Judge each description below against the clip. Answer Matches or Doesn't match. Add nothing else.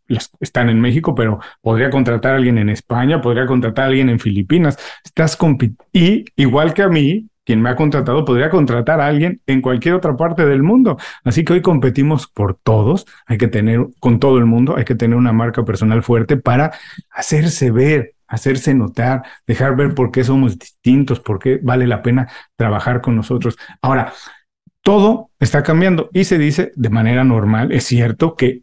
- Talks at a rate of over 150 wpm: Matches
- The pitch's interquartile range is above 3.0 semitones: Matches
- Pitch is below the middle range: Matches